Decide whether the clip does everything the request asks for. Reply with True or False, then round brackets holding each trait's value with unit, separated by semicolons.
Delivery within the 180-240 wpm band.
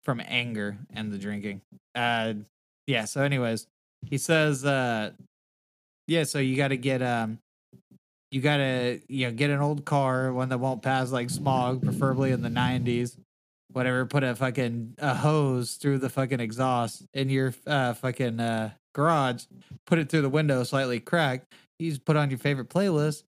False (170 wpm)